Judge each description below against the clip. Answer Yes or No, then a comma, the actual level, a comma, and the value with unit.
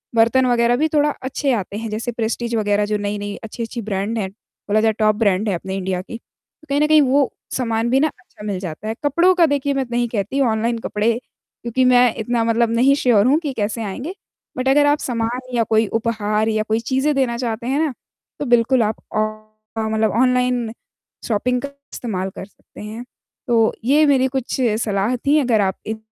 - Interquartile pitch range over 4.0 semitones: No, average, 3.3 semitones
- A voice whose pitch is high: Yes, high, 230 Hz